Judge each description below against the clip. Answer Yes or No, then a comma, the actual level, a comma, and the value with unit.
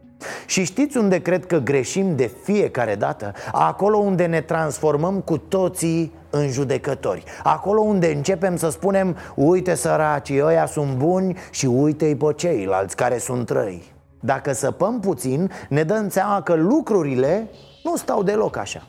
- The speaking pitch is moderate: Yes, medium, 170 Hz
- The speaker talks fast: No, average, 145 wpm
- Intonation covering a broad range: No, average, 4.8 semitones